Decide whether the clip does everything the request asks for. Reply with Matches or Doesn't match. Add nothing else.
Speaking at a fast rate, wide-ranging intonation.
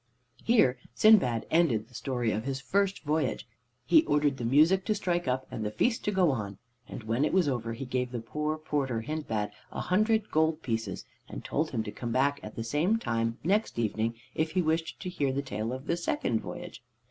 Matches